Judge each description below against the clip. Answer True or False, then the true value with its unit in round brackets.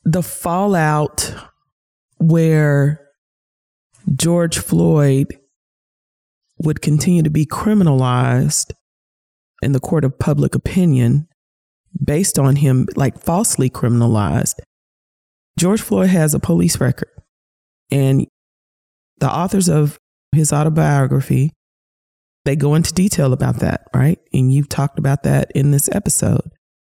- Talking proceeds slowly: True (110 wpm)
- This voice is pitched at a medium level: True (145 Hz)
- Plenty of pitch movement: False (3.5 semitones)